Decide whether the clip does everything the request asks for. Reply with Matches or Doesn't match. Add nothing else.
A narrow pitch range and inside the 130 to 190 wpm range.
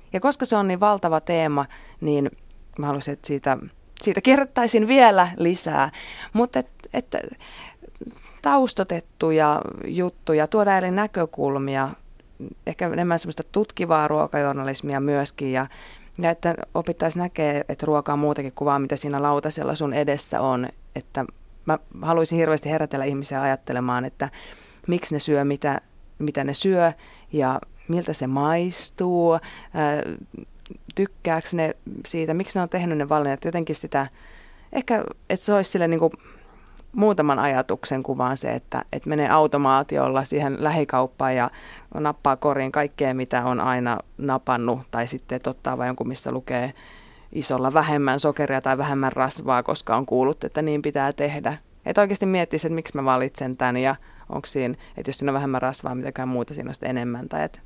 Doesn't match